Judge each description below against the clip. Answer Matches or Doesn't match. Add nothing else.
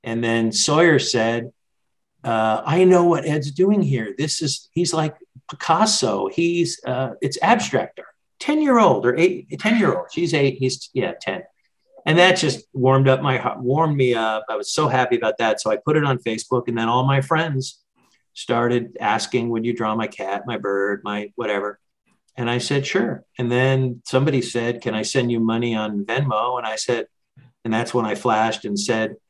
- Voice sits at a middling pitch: Doesn't match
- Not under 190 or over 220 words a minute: Matches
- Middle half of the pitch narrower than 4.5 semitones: Doesn't match